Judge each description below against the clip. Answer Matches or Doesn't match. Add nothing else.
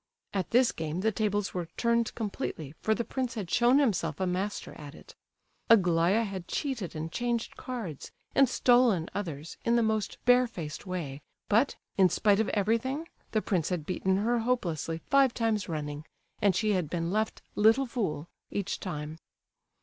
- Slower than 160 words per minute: Doesn't match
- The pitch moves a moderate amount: Doesn't match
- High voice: Matches